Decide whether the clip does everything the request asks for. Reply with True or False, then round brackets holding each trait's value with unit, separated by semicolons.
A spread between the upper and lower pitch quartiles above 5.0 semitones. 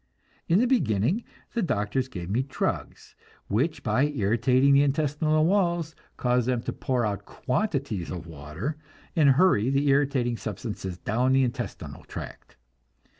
True (5.5 semitones)